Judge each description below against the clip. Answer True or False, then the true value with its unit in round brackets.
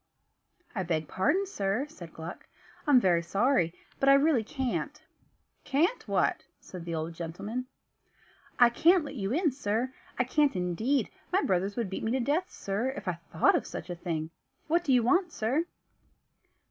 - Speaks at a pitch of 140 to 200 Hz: False (235 Hz)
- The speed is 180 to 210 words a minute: False (170 wpm)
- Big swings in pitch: True (7.9 semitones)